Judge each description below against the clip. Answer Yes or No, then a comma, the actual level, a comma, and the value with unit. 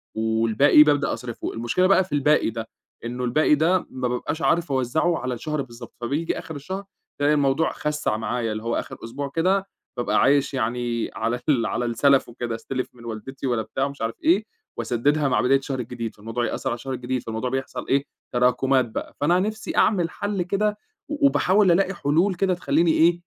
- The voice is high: No, low, 135 Hz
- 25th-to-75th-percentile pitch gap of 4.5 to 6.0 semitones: Yes, wide, 5.4 semitones